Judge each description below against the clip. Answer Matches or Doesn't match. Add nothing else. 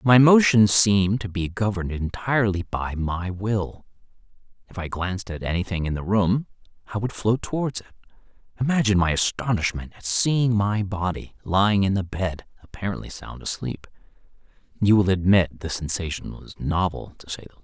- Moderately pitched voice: Doesn't match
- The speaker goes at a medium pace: Matches